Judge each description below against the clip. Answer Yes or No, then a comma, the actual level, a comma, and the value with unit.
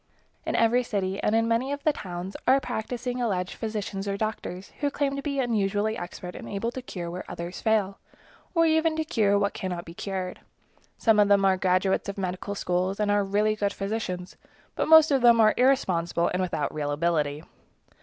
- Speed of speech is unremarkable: Yes, average, 195 wpm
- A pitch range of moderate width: Yes, average, 4.4 semitones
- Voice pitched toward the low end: No, high, 205 Hz